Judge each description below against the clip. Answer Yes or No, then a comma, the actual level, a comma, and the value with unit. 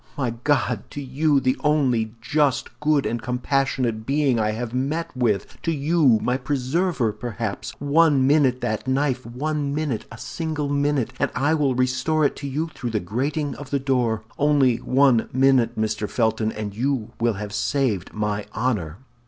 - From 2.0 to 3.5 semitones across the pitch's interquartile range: No, average, 4.0 semitones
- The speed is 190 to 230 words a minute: No, average, 160 wpm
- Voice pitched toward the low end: Yes, low, 130 Hz